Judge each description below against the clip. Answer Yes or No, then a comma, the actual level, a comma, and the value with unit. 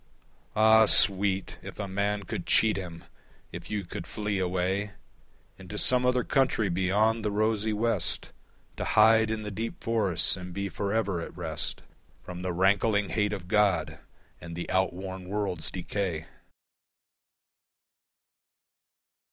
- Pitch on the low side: Yes, low, 100 Hz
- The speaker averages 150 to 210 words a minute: No, slow, 135 wpm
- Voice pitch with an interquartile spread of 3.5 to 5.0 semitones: No, average, 2.8 semitones